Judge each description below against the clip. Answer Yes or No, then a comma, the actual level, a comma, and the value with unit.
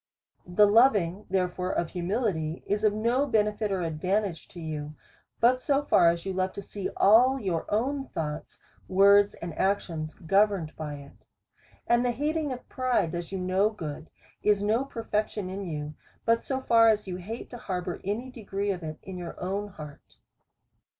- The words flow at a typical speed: Yes, average, 175 wpm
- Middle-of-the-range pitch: No, high, 195 Hz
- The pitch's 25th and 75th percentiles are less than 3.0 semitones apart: No, average, 4.6 semitones